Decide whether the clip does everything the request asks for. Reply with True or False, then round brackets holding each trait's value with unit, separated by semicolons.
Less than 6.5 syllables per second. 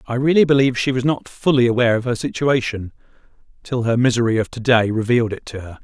False (6.6 syllables/s)